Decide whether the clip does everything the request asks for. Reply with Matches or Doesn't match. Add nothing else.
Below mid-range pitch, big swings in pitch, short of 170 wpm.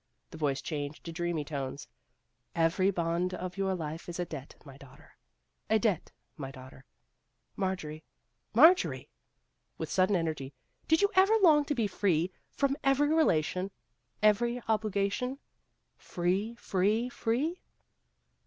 Doesn't match